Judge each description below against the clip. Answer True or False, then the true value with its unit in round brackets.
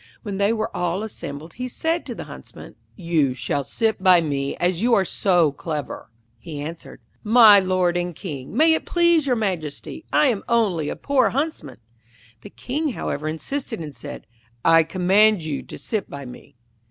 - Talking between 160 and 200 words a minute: True (175 wpm)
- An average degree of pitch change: False (6.7 semitones)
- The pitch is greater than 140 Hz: True (185 Hz)